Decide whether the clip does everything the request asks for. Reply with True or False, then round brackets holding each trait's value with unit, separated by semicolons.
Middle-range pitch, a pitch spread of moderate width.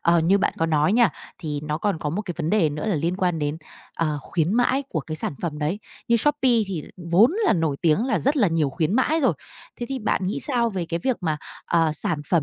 False (175 Hz; 6.1 semitones)